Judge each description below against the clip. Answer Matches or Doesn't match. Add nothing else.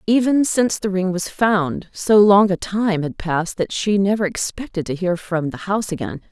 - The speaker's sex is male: Doesn't match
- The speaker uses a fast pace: Matches